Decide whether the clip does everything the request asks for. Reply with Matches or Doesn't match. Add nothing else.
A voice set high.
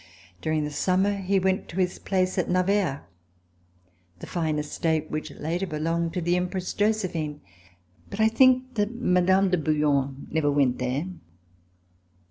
Doesn't match